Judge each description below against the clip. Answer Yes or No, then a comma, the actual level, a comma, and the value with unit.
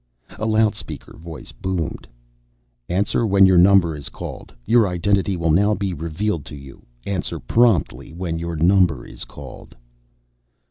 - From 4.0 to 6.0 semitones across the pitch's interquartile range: No, average, 3.6 semitones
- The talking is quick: No, average, 140 wpm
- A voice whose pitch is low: Yes, very low, 90 Hz